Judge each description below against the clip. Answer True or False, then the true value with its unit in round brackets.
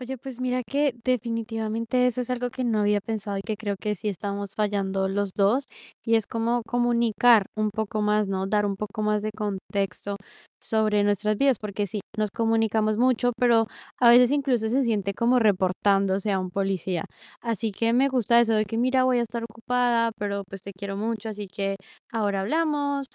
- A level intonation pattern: False (3.0 semitones)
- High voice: True (220 Hz)